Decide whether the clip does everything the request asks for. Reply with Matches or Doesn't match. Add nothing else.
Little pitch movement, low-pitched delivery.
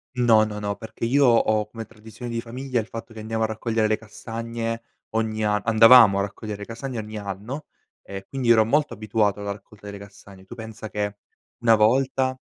Matches